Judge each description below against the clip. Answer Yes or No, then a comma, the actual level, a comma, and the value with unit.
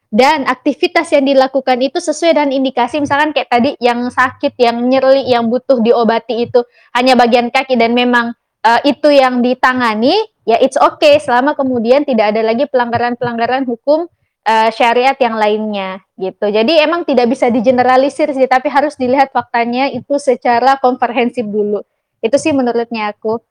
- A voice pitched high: Yes, very high, 250 Hz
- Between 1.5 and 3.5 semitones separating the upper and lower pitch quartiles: Yes, average, 2.7 semitones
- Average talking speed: No, fast, 155 wpm